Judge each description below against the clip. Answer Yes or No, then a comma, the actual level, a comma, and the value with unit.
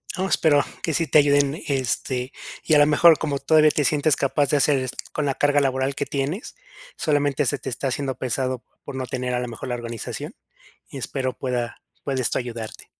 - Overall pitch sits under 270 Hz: Yes, medium, 140 Hz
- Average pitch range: No, narrow, 2.2 semitones